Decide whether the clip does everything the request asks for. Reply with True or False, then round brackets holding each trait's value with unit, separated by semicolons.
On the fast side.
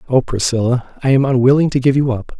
True (225 wpm)